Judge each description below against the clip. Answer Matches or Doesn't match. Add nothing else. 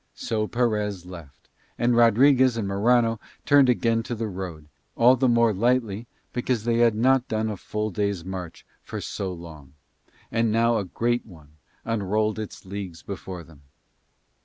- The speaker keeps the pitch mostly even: Doesn't match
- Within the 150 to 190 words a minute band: Matches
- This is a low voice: Matches